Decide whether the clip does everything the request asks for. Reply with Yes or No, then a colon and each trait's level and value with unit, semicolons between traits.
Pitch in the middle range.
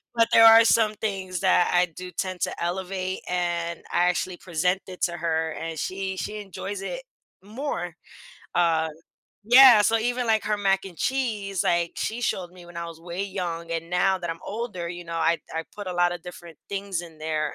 Yes: medium, 180 Hz